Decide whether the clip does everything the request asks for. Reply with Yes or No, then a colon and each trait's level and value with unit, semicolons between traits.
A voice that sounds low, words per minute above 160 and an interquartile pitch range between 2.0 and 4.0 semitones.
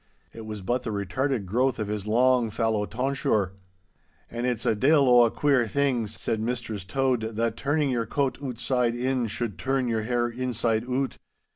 Yes: low, 120 Hz; average, 175 wpm; average, 2.8 semitones